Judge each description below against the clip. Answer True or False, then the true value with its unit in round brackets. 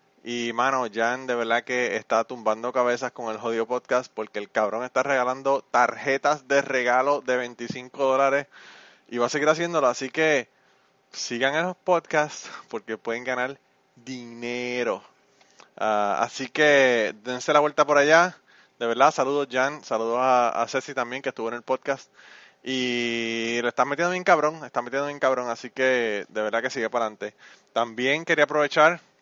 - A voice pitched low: True (125 Hz)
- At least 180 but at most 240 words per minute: False (170 wpm)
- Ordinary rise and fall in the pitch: True (3.1 semitones)